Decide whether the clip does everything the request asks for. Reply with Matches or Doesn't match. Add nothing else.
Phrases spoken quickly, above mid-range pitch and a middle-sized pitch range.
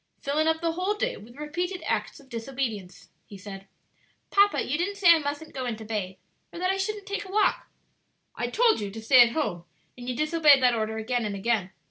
Doesn't match